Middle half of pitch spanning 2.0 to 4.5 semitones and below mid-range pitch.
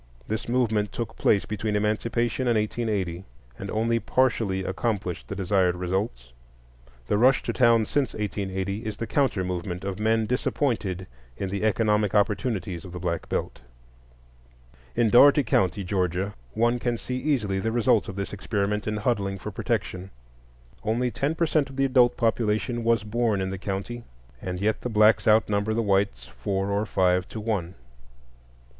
Yes: average, 3.4 semitones; low, 105 Hz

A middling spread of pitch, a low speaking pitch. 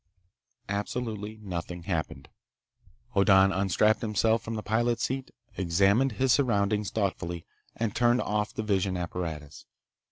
Yes: average, 3.5 semitones; low, 100 Hz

